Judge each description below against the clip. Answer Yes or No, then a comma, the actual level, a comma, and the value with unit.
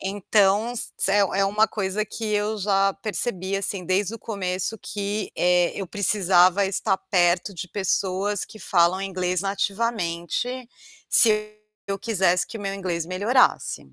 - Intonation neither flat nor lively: No, narrow, 2.3 semitones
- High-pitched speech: Yes, high, 195 Hz